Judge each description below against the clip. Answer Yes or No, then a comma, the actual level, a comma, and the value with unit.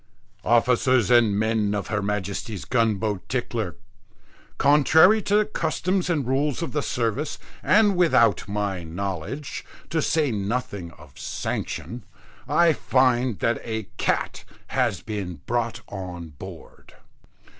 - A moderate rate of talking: No, slow, 125 wpm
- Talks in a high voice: No, low, 115 Hz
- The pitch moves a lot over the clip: Yes, wide, 6.1 semitones